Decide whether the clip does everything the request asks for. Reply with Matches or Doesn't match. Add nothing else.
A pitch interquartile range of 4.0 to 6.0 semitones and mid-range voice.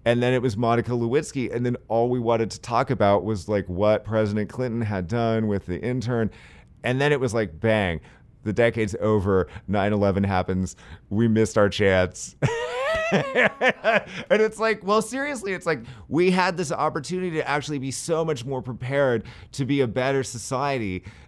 Doesn't match